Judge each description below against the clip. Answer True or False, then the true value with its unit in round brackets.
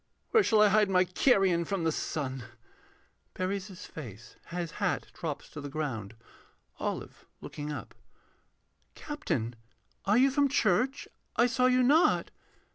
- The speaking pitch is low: False (185 Hz)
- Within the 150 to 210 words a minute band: False (140 wpm)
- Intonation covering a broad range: True (8.5 semitones)